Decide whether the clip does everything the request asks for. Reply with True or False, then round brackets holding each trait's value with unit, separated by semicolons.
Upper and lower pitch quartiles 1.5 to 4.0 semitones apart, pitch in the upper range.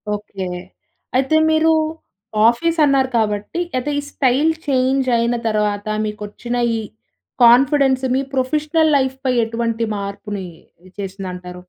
False (4.7 semitones; 245 Hz)